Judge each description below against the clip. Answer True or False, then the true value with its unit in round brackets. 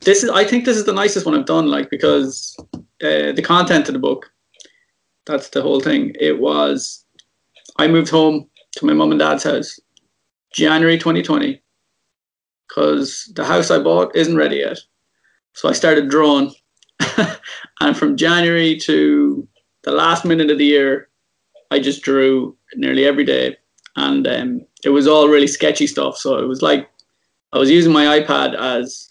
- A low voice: False (155 Hz)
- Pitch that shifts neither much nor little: False (5.8 semitones)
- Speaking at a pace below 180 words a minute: True (170 wpm)